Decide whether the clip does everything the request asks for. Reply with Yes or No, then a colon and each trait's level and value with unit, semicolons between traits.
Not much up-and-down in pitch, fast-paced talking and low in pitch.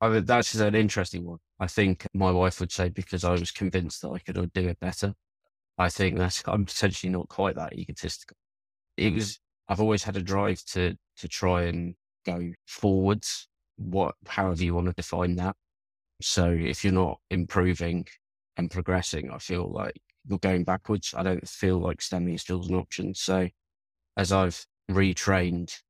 No: narrow, 1.7 semitones; average, 180 wpm; very low, 90 Hz